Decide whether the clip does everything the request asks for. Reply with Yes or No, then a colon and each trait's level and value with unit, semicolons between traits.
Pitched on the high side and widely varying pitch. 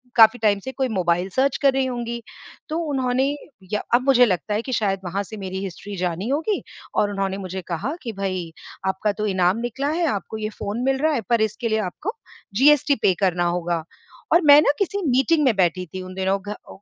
Yes: high, 215 Hz; wide, 5.7 semitones